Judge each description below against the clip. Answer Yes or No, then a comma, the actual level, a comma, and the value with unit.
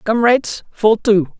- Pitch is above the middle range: Yes, high, 220 Hz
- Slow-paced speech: Yes, slow, 130 wpm